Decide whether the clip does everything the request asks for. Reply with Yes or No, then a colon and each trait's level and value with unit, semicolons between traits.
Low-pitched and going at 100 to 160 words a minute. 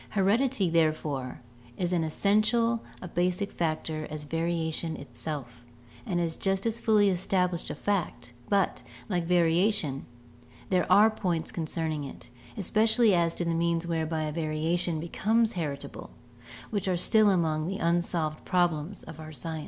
No: medium, 170 Hz; average, 145 wpm